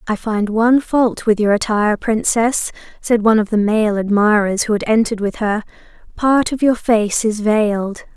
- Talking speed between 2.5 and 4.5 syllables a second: No, 5.0 syllables/s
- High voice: Yes, high, 215 Hz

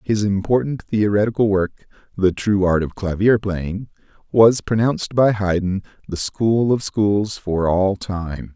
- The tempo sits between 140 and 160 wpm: Yes, average, 145 wpm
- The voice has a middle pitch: No, low, 100 Hz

